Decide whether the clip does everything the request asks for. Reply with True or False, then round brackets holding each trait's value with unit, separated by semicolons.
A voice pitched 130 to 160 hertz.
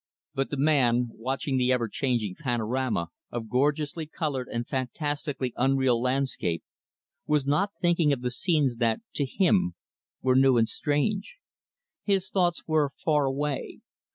True (135 Hz)